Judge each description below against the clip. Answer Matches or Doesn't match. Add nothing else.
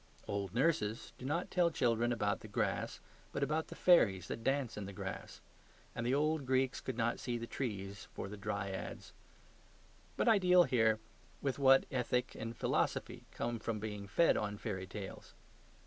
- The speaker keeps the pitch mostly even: Doesn't match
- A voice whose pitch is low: Matches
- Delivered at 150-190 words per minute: Matches